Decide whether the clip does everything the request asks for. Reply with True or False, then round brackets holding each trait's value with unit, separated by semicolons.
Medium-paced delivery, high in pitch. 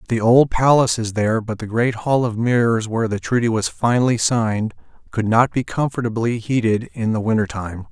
False (195 wpm; 115 Hz)